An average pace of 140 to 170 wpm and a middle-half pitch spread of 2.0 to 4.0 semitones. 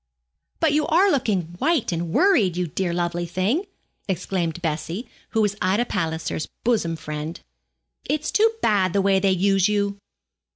No: average, 155 wpm; average, 5.3 semitones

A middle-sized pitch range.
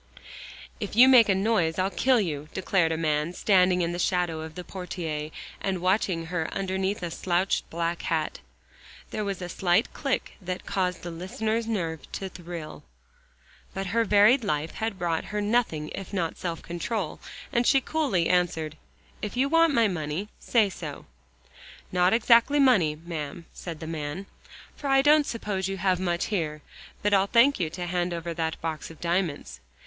Yes: average, 4.1 semitones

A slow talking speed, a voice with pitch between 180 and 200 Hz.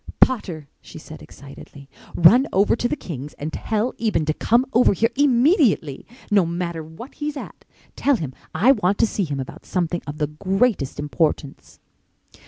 No: average, 165 wpm; medium, 185 Hz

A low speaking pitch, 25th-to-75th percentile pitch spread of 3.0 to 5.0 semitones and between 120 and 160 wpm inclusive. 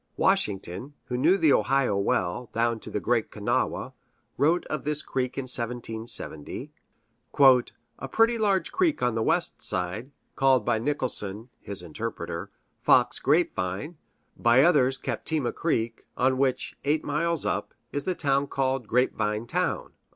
Yes: low, 125 Hz; average, 4.5 semitones; average, 145 wpm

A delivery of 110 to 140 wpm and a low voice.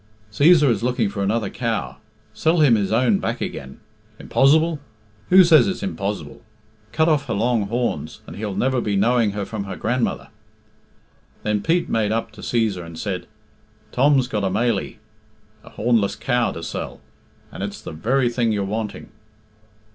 No: average, 160 wpm; low, 115 Hz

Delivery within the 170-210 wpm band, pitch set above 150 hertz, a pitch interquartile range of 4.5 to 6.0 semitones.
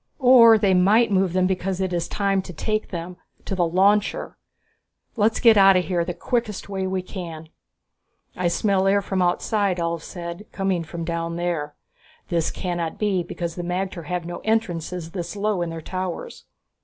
No: average, 180 wpm; medium, 185 Hz; narrow, 2.6 semitones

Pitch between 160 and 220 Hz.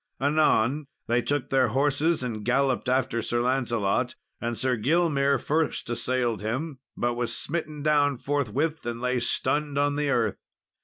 No: low, 130 Hz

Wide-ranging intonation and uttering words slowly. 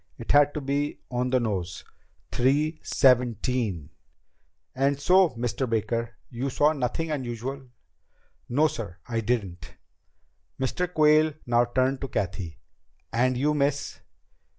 No: average, 3.7 semitones; slow, 125 wpm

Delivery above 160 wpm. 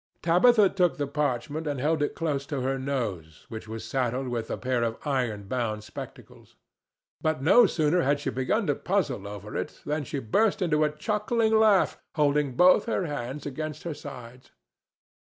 Yes: average, 175 wpm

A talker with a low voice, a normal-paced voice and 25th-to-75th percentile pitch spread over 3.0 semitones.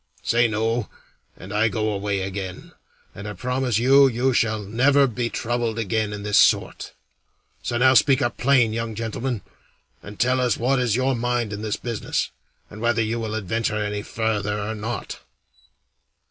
No: low, 115 Hz; average, 170 wpm; average, 2.7 semitones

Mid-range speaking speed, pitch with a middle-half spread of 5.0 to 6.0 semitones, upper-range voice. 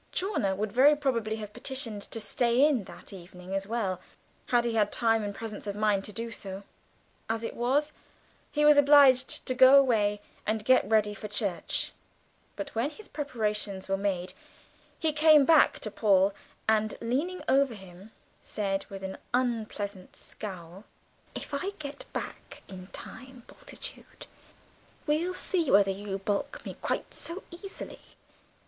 Yes: average, 155 wpm; average, 5.3 semitones; high, 220 Hz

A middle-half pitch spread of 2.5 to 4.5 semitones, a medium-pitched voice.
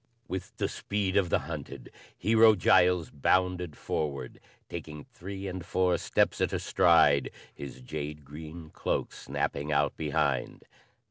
No: average, 3.9 semitones; very low, 85 Hz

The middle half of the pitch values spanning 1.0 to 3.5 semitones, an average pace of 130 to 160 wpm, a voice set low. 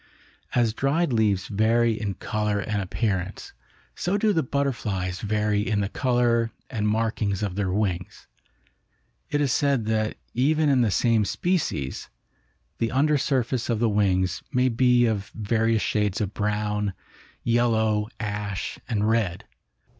Yes: average, 3.0 semitones; average, 140 wpm; low, 110 Hz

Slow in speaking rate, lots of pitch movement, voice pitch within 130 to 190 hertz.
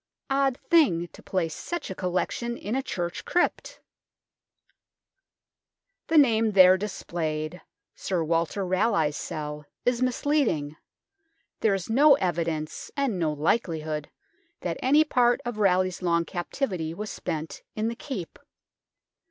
Yes: slow, 125 wpm; wide, 6.6 semitones; medium, 185 Hz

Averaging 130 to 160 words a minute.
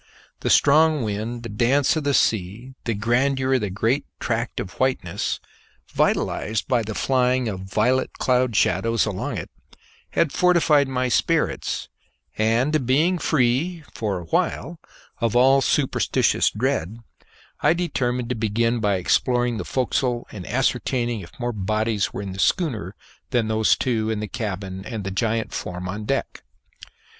Yes: average, 150 wpm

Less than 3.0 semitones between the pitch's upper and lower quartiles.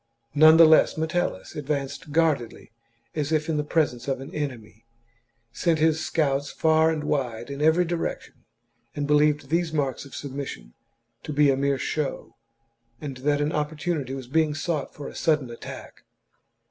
Yes: narrow, 2.5 semitones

